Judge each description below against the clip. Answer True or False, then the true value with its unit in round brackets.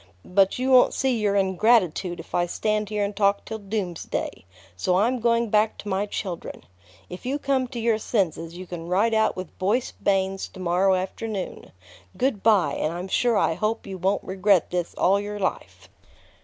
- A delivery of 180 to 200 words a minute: True (185 wpm)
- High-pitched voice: True (200 Hz)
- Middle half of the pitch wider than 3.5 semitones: False (3.2 semitones)